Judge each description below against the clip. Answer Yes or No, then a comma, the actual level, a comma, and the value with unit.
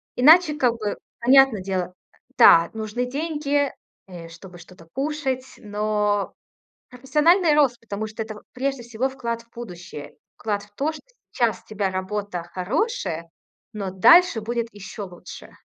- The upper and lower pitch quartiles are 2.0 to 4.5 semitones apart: No, wide, 5.6 semitones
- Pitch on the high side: Yes, high, 225 Hz